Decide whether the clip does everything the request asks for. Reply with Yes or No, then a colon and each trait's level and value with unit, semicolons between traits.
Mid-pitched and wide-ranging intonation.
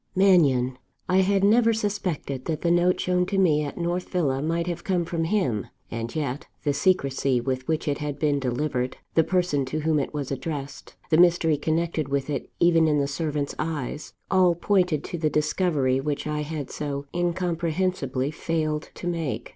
No: medium, 155 Hz; average, 3.8 semitones